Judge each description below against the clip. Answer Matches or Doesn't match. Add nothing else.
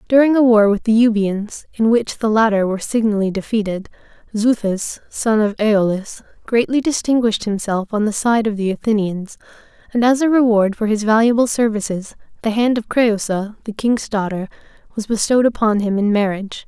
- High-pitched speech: Matches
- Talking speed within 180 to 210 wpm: Doesn't match